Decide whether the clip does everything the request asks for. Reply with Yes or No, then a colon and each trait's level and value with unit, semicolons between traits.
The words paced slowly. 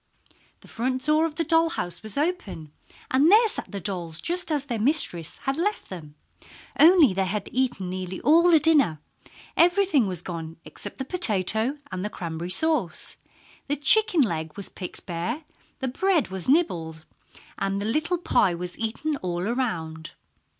No: average, 170 wpm